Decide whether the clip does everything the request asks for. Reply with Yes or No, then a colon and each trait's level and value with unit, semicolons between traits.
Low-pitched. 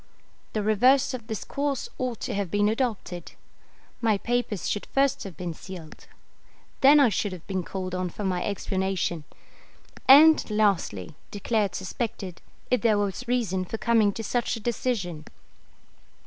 No: high, 210 Hz